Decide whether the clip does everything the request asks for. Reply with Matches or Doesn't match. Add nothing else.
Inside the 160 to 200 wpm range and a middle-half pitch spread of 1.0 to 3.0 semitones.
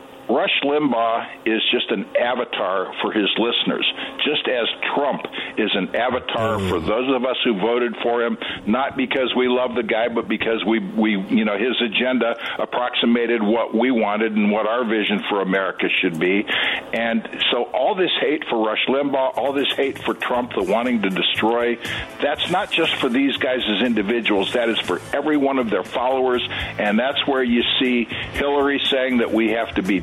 Matches